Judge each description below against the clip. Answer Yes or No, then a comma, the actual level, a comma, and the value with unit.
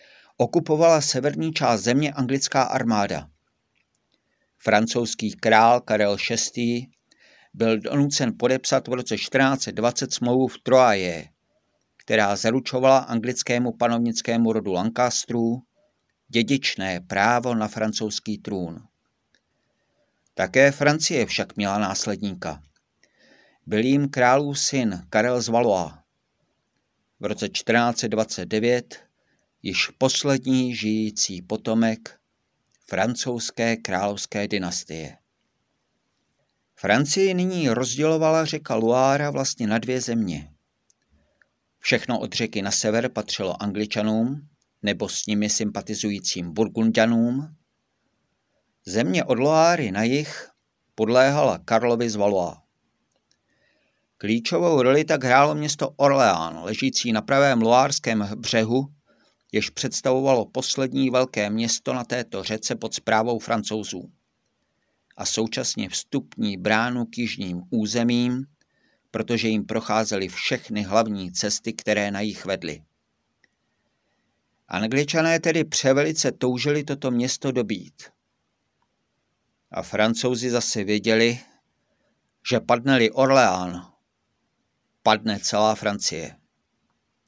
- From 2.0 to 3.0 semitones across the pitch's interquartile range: No, average, 3.6 semitones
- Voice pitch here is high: No, low, 115 Hz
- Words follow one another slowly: Yes, slow, 95 wpm